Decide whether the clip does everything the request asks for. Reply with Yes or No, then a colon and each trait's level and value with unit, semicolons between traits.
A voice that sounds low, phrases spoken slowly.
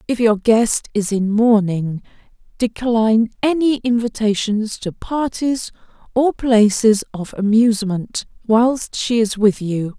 No: high, 220 Hz; slow, 120 wpm